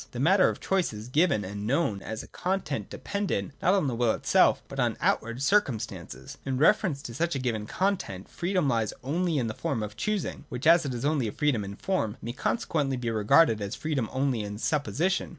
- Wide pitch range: Yes, wide, 7.2 semitones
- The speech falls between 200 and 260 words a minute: Yes, fast, 205 wpm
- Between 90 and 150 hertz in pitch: Yes, low, 135 Hz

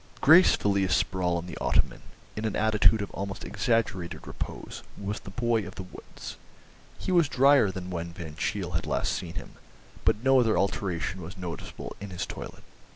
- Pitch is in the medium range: No, low, 100 Hz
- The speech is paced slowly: No, average, 175 wpm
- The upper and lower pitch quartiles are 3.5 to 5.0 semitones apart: Yes, average, 3.8 semitones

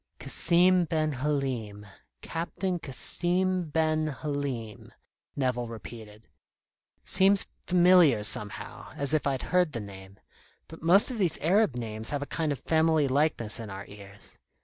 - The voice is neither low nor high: Yes, medium, 145 Hz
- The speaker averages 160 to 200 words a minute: No, slow, 135 wpm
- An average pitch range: No, wide, 7.0 semitones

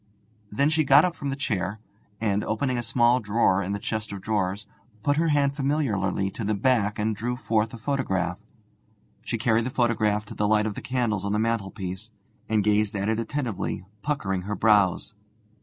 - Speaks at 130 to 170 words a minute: No, average, 190 wpm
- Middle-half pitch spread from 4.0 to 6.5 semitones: No, average, 3.6 semitones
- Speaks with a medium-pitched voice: No, low, 110 Hz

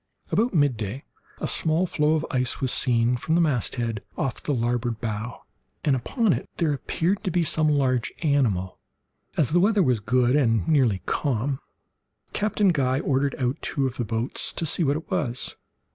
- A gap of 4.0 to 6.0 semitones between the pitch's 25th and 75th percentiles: Yes, average, 4.6 semitones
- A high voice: No, low, 135 Hz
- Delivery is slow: No, average, 175 wpm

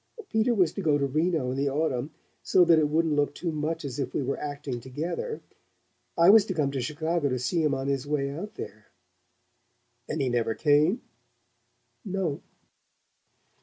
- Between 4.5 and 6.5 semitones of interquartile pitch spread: No, average, 3.4 semitones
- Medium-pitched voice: Yes, medium, 150 Hz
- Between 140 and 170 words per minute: No, average, 180 wpm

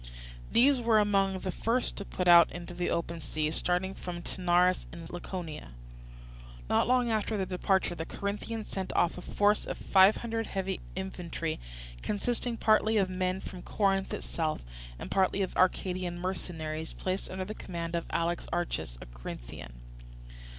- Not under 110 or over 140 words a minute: No, average, 155 wpm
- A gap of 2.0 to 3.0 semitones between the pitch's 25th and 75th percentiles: Yes, average, 2.7 semitones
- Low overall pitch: No, medium, 185 Hz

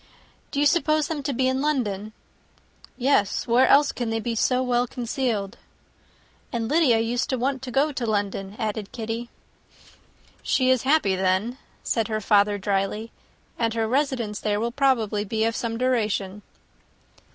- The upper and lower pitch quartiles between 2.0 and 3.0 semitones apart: No, average, 3.6 semitones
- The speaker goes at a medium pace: Yes, average, 160 wpm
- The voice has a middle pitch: No, high, 235 Hz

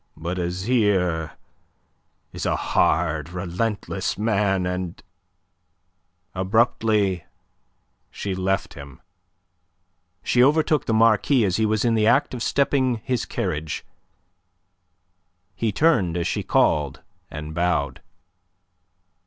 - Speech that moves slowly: Yes, slow, 105 wpm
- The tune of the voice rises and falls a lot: No, average, 4.7 semitones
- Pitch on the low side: Yes, very low, 95 Hz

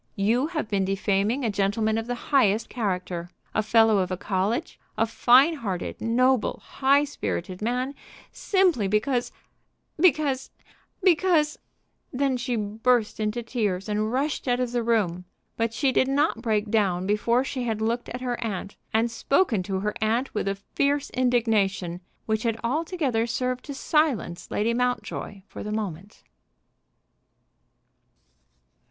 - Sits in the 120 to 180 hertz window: No, high, 230 Hz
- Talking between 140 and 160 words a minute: Yes, average, 145 wpm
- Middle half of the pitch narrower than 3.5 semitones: No, average, 3.8 semitones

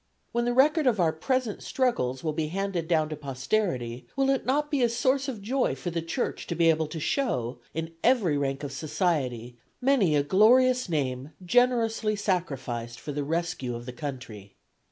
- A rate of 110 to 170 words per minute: No, average, 185 wpm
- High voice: No, medium, 165 Hz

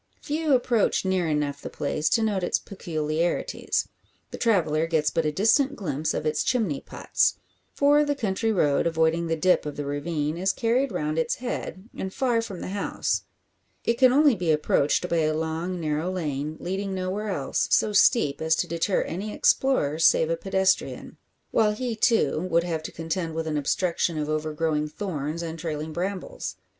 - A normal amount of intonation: Yes, average, 4.9 semitones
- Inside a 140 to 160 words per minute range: No, average, 180 wpm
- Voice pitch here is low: No, medium, 170 Hz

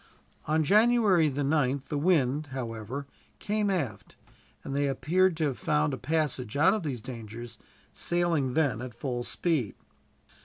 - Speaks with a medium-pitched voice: Yes, medium, 145 Hz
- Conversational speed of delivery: Yes, average, 150 wpm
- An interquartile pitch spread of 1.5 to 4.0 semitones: No, average, 4.5 semitones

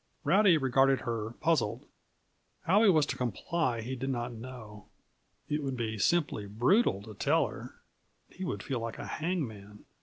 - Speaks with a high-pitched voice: No, low, 125 Hz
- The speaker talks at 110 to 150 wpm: No, average, 160 wpm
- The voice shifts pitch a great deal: Yes, wide, 5.9 semitones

